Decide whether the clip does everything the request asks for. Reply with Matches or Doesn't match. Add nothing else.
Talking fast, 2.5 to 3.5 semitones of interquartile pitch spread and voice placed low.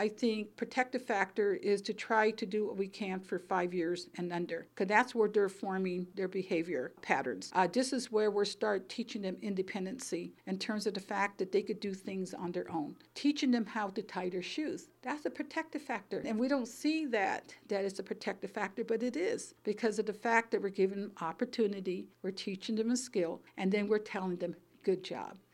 Doesn't match